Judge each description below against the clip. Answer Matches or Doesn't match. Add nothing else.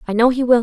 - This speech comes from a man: Doesn't match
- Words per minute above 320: Matches